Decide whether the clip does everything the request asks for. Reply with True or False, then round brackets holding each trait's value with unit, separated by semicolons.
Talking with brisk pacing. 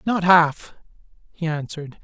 False (120 wpm)